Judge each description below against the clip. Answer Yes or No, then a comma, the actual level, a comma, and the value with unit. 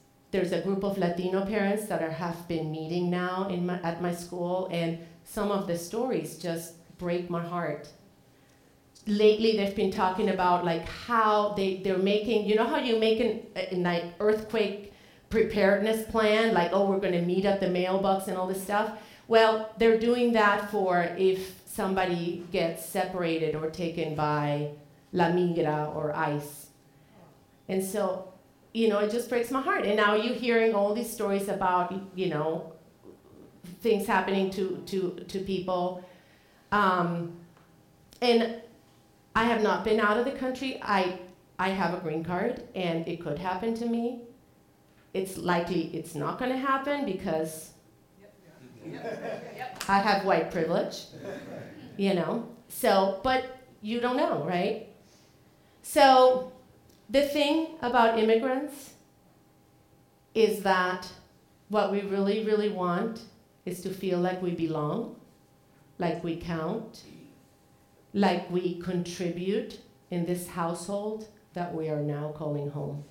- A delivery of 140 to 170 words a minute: Yes, average, 145 wpm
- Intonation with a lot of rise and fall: No, average, 3.9 semitones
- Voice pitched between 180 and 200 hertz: Yes, high, 190 Hz